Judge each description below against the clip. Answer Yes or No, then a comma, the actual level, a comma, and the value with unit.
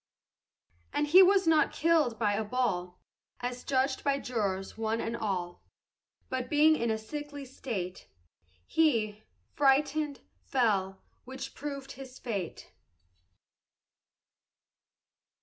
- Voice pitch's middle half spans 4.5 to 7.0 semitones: Yes, average, 5.2 semitones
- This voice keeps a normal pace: No, slow, 110 wpm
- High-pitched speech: Yes, very high, 250 Hz